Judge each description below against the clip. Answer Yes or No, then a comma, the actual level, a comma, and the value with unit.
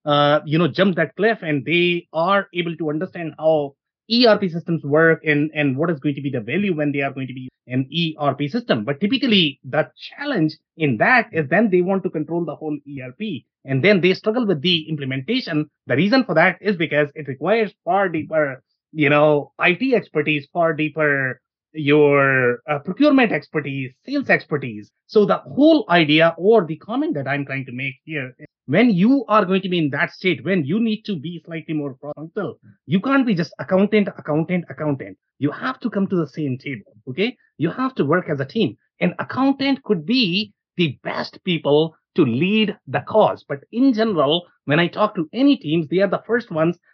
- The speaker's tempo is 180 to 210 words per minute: Yes, average, 200 wpm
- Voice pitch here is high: No, medium, 165 Hz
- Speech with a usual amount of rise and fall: No, wide, 5.7 semitones